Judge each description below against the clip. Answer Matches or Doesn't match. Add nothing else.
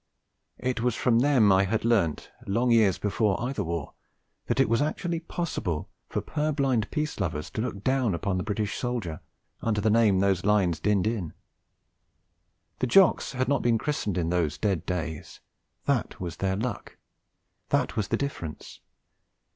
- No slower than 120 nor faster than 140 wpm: Doesn't match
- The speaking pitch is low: Matches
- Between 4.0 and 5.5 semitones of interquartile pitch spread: Matches